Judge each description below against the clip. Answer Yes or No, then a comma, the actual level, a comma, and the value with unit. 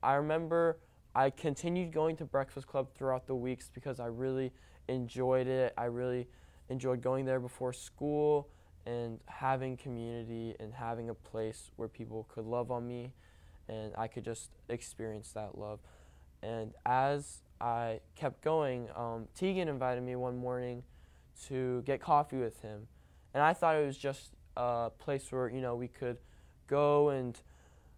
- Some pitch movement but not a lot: Yes, average, 3.1 semitones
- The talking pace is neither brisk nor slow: Yes, average, 160 wpm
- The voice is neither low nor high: No, low, 125 Hz